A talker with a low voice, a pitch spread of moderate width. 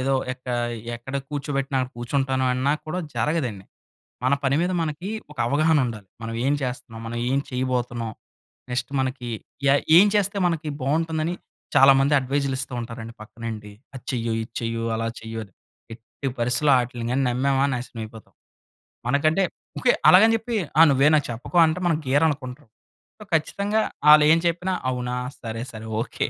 Yes: low, 130 Hz; average, 4.3 semitones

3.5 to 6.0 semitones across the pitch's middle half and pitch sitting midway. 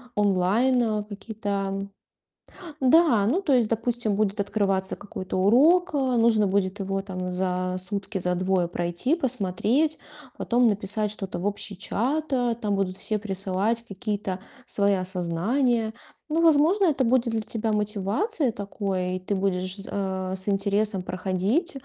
No: average, 4.0 semitones; high, 205 Hz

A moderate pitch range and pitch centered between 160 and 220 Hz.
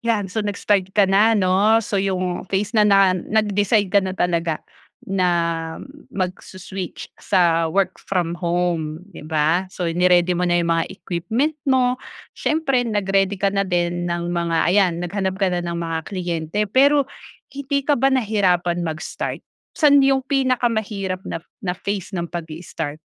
Yes: average, 3.3 semitones; high, 190 Hz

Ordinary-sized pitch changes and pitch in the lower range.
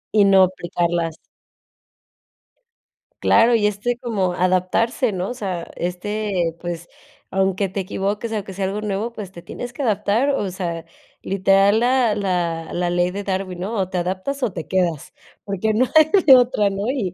No: average, 3.4 semitones; high, 195 Hz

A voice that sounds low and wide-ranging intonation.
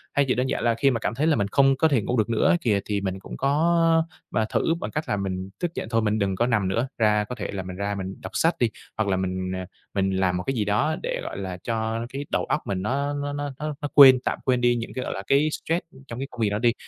Yes: low, 115 Hz; wide, 5.8 semitones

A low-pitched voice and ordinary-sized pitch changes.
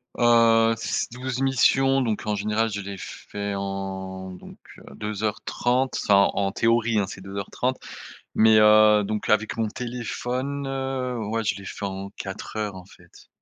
Yes: low, 110 Hz; average, 3.6 semitones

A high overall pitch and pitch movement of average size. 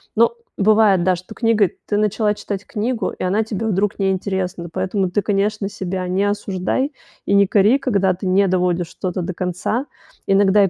No: high, 195 Hz; narrow, 2.3 semitones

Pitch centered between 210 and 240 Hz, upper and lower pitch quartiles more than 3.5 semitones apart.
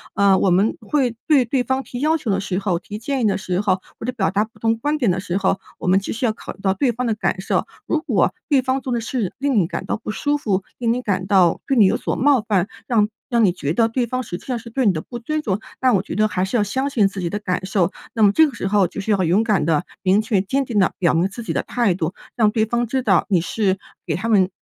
Yes: high, 215 Hz; average, 4.5 semitones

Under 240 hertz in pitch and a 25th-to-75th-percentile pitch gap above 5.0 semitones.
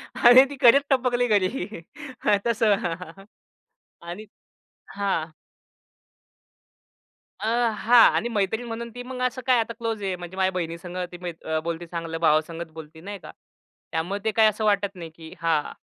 Yes: high, 195 Hz; wide, 5.5 semitones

